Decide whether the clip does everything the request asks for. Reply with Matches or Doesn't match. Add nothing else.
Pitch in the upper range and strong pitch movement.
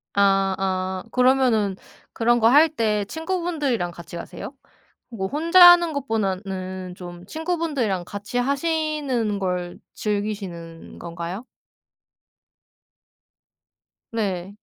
Matches